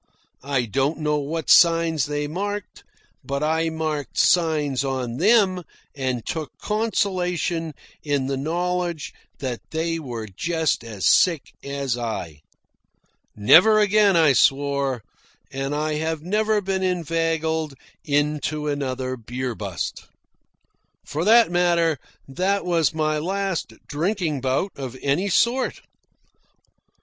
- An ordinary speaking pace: No, slow, 120 wpm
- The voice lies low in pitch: No, medium, 155 Hz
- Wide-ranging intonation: No, average, 4.5 semitones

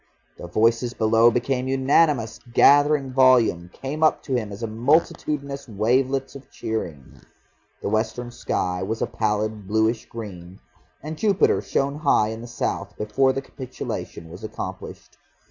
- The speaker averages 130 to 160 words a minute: Yes, average, 140 wpm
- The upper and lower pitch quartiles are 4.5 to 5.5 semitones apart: No, average, 3.9 semitones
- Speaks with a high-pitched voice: No, low, 120 Hz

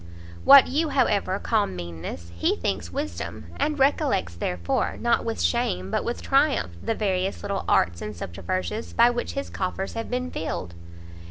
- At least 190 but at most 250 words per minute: No, average, 160 wpm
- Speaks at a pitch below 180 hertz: No, medium, 185 Hz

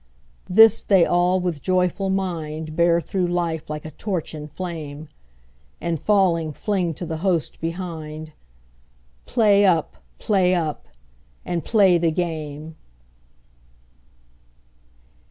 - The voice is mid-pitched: Yes, medium, 170 Hz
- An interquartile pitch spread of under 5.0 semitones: Yes, average, 2.8 semitones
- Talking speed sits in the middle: No, slow, 120 wpm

